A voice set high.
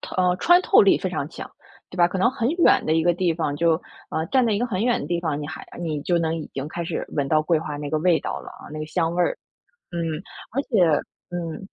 No: medium, 170 Hz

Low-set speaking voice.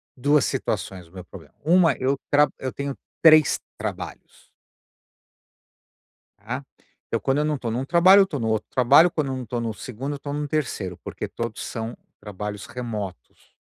Yes: low, 130 Hz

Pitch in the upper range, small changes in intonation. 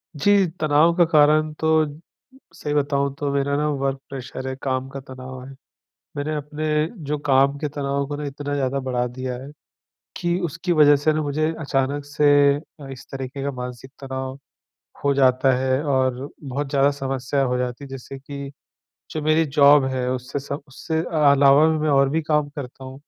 No: medium, 140 Hz; narrow, 1.9 semitones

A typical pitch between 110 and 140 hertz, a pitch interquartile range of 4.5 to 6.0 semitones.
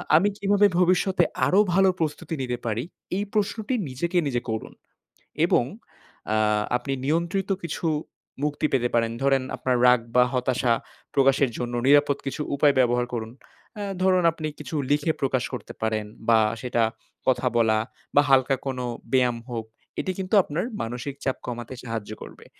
Yes: low, 135 Hz; average, 4.9 semitones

